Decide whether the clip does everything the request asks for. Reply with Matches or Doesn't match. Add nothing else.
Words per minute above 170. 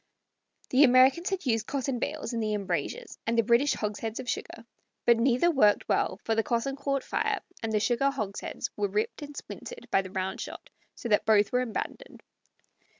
Matches